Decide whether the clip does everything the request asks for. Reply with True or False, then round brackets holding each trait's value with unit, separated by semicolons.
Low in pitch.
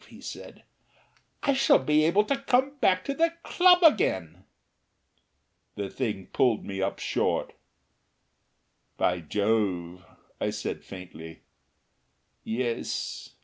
True (120 Hz)